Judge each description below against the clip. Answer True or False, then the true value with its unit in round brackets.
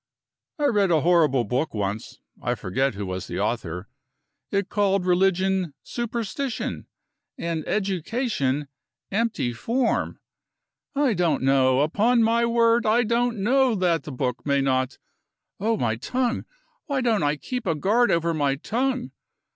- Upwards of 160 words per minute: False (140 wpm)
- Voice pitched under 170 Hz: False (190 Hz)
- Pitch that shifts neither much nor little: False (9.0 semitones)